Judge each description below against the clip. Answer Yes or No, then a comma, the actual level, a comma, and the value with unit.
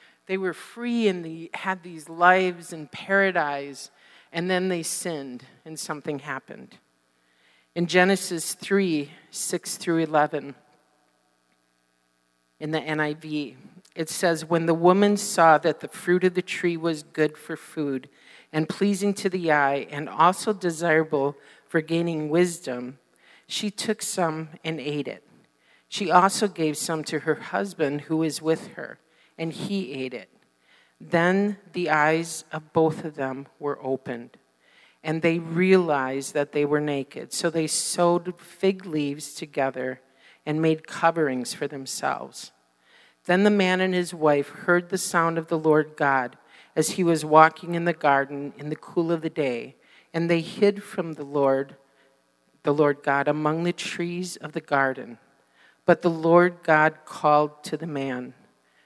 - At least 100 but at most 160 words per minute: Yes, average, 155 wpm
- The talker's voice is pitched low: No, medium, 160 Hz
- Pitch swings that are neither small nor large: Yes, average, 3.4 semitones